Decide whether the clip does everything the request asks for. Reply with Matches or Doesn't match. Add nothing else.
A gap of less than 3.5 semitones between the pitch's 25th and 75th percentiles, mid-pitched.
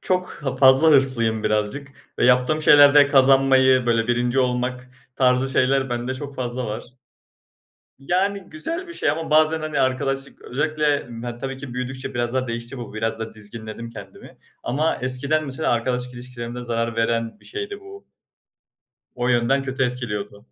Doesn't match